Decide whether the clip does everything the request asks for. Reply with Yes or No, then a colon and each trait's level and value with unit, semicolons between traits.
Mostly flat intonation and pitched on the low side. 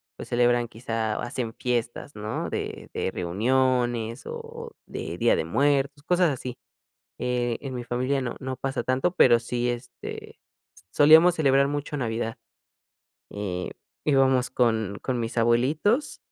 No: average, 3.0 semitones; low, 125 Hz